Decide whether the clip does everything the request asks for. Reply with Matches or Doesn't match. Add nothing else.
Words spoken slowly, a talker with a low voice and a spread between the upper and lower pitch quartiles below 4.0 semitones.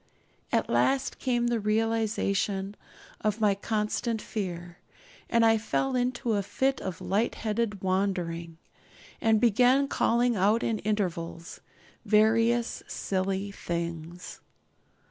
Doesn't match